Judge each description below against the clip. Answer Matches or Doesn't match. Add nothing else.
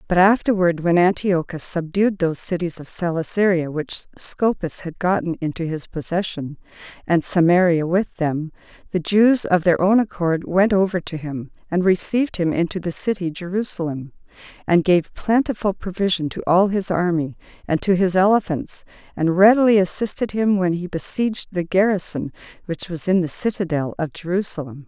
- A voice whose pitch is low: Doesn't match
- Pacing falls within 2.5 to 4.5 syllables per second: Doesn't match